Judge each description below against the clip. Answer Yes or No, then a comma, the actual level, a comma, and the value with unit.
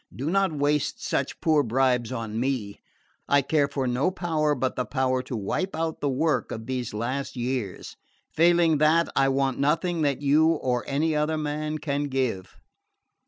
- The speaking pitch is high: No, medium, 140 Hz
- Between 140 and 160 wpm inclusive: No, average, 170 wpm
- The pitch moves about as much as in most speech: Yes, average, 3.3 semitones